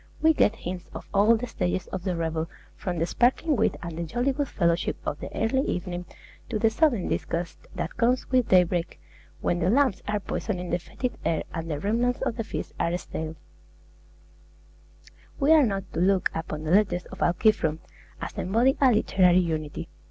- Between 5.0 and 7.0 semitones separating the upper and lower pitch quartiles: Yes, wide, 5.4 semitones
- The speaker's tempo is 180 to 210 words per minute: Yes, average, 185 wpm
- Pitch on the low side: No, high, 190 Hz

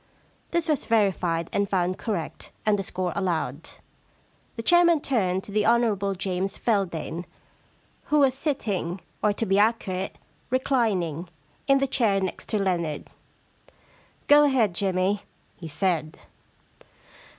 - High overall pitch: Yes, high, 195 Hz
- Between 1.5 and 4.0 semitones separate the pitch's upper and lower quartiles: No, average, 4.5 semitones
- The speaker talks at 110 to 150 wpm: Yes, average, 140 wpm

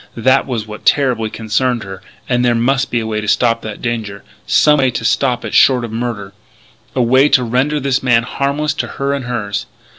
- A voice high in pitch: No, low, 120 Hz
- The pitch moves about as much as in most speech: Yes, average, 3.2 semitones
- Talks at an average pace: No, fast, 210 wpm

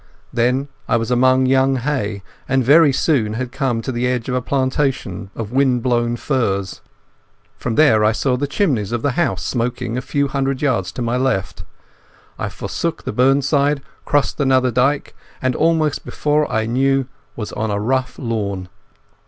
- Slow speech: No, average, 170 wpm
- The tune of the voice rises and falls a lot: No, average, 2.9 semitones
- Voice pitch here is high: No, low, 125 Hz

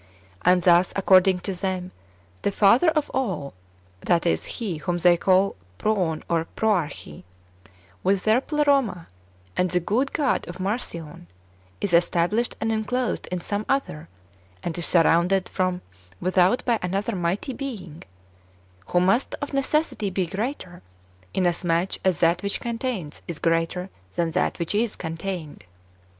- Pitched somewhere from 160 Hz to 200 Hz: Yes, medium, 185 Hz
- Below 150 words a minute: Yes, average, 140 wpm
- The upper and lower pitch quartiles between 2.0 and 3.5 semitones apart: No, average, 4.1 semitones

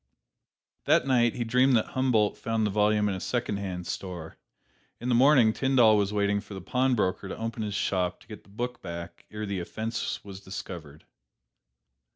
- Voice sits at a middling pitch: No, low, 105 Hz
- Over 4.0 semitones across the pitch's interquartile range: No, average, 3.7 semitones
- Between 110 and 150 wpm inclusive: No, average, 180 wpm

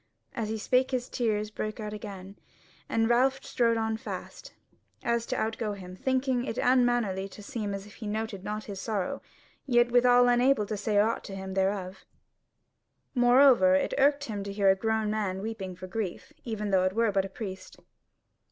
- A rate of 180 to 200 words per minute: Yes, average, 190 wpm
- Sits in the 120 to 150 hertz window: No, high, 220 Hz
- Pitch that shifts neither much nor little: Yes, average, 3.5 semitones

